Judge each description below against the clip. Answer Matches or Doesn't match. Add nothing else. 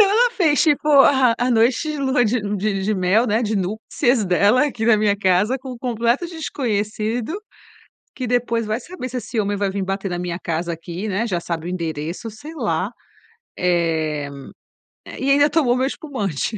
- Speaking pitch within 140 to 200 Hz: Doesn't match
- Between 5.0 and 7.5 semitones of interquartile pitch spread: Matches